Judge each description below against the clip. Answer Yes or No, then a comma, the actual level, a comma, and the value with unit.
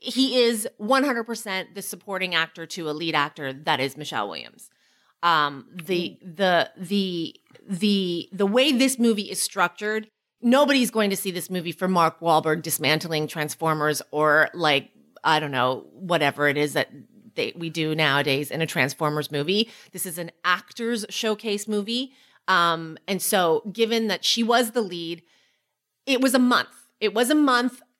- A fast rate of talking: No, average, 165 wpm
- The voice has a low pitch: No, medium, 185 Hz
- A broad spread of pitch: Yes, wide, 6.3 semitones